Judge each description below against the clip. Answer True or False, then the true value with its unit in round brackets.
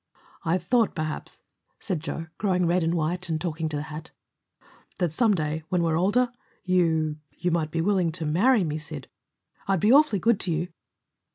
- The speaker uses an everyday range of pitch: True (3.1 semitones)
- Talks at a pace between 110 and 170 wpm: False (185 wpm)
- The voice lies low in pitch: False (170 Hz)